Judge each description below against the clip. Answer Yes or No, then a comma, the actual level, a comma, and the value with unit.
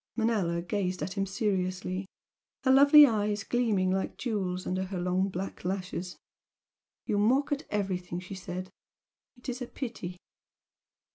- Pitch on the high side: Yes, high, 195 Hz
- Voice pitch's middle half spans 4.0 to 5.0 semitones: No, average, 3.5 semitones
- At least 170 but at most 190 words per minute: No, average, 140 wpm